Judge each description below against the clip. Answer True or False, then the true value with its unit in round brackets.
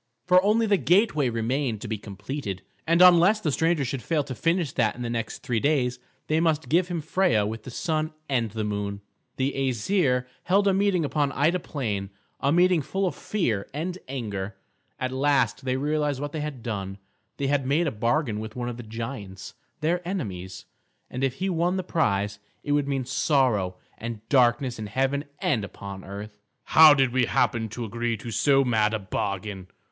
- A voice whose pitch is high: False (130 Hz)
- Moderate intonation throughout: False (6.2 semitones)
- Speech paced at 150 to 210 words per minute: True (190 wpm)